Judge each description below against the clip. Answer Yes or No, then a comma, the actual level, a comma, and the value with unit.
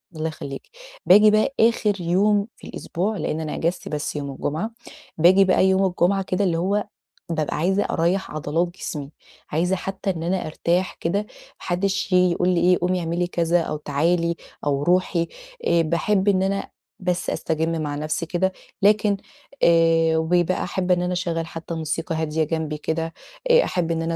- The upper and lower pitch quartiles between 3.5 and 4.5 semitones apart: No, narrow, 2.6 semitones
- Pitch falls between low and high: Yes, medium, 175 Hz